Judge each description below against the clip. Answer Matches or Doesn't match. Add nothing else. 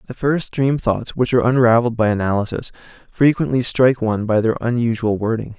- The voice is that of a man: Matches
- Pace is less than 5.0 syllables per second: Doesn't match